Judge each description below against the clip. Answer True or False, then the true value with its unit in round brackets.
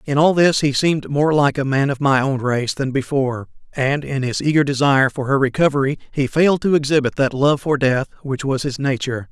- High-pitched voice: False (140 Hz)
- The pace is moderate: False (225 wpm)